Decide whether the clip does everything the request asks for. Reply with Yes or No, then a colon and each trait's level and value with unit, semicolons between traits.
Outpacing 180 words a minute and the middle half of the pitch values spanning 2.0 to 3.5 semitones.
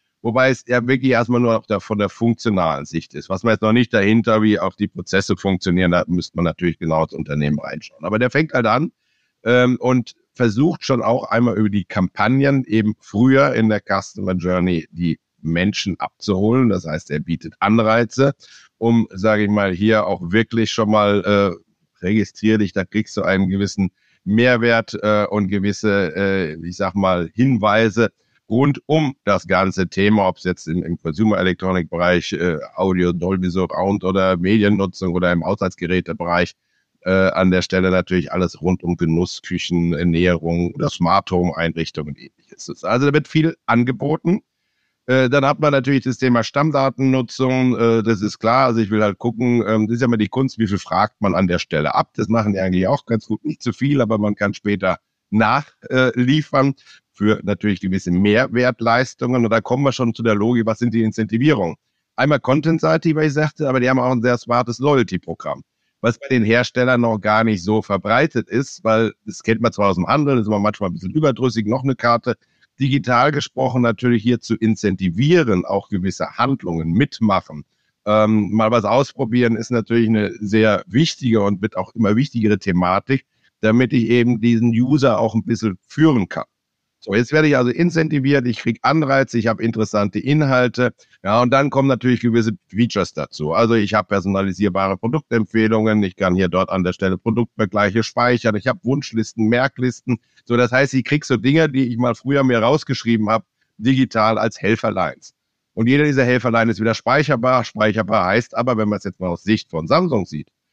No: fast, 190 wpm; average, 4.2 semitones